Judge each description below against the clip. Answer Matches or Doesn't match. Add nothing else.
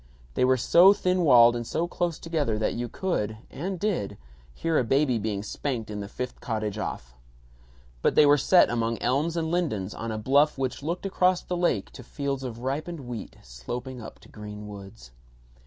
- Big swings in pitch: Matches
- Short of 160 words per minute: Doesn't match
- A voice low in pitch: Matches